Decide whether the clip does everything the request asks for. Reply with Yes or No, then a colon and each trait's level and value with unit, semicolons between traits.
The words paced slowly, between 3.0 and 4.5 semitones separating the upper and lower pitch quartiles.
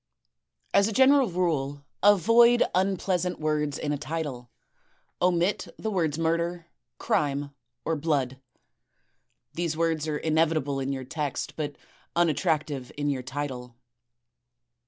Yes: slow, 115 wpm; average, 3.5 semitones